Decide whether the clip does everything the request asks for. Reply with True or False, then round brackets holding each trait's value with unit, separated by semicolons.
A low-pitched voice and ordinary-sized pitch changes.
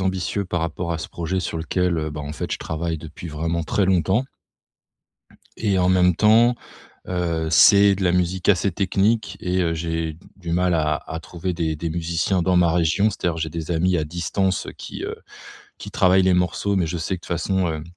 False (85 Hz; 2.3 semitones)